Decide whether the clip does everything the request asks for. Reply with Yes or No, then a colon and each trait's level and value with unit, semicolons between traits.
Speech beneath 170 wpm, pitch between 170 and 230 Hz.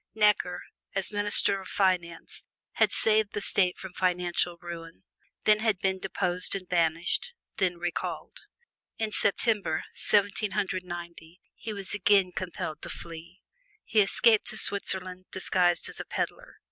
Yes: average, 140 wpm; medium, 185 Hz